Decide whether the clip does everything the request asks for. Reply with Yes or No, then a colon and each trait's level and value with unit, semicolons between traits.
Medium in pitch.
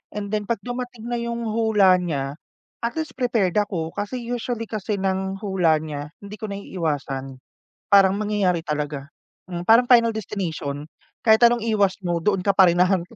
No: high, 200 Hz